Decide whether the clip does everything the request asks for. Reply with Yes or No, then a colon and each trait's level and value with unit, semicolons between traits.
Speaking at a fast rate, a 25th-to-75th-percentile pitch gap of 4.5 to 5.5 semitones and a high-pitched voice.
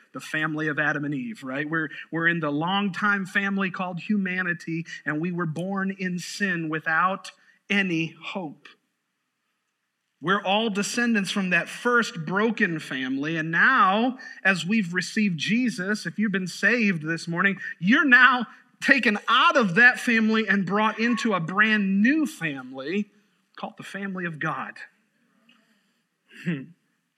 No: average, 140 wpm; average, 4.8 semitones; high, 195 Hz